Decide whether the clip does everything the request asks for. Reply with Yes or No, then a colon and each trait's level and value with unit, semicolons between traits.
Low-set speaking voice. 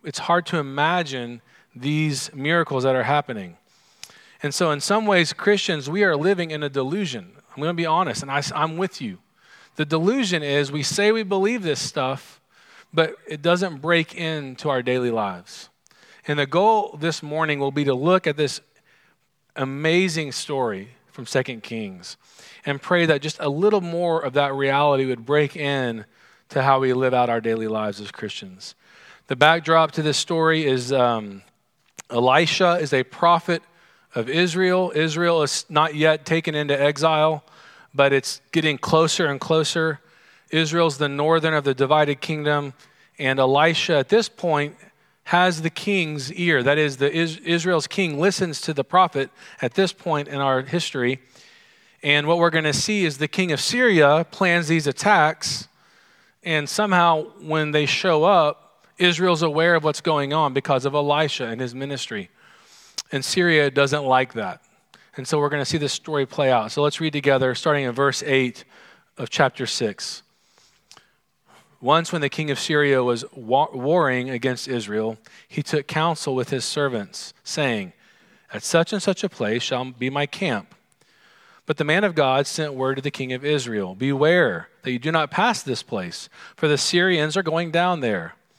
No: medium, 150 Hz